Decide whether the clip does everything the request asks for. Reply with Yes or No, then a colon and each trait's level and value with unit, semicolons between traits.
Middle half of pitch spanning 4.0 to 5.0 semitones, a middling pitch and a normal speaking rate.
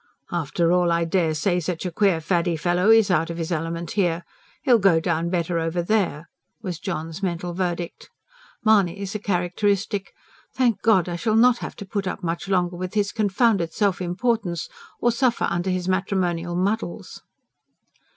No: average, 2.9 semitones; medium, 180 Hz; average, 170 wpm